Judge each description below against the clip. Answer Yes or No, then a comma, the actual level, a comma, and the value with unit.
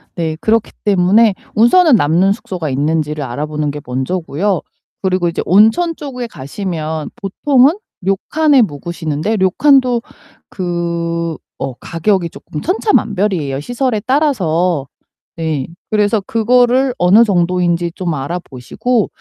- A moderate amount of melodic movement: No, wide, 6.2 semitones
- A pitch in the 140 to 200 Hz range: Yes, medium, 185 Hz